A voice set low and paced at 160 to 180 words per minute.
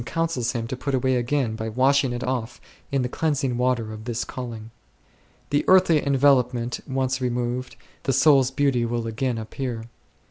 Yes: low, 125 Hz; average, 165 wpm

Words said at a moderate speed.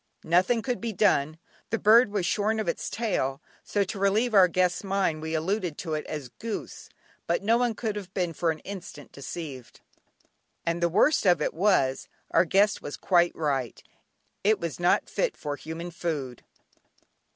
Yes: average, 175 wpm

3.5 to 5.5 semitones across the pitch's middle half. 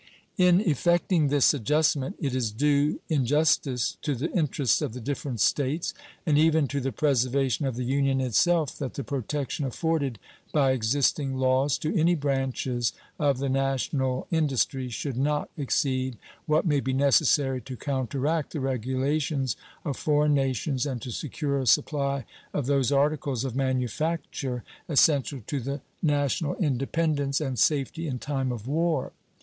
No: narrow, 2.4 semitones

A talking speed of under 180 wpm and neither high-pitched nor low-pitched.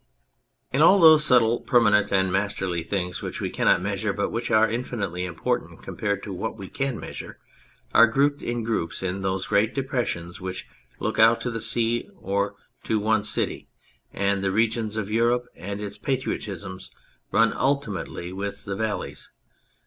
No: average, 155 wpm; low, 105 Hz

